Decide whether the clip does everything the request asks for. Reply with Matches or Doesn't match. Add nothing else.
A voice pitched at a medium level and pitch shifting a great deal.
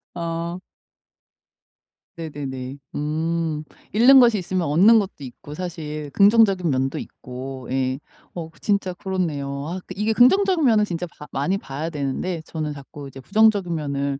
Matches